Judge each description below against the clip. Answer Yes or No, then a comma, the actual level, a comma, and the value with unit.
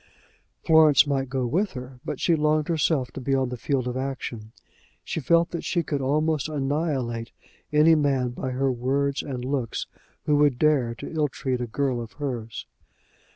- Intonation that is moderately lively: Yes, average, 3.3 semitones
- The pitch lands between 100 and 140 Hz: Yes, low, 135 Hz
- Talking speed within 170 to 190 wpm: Yes, average, 180 wpm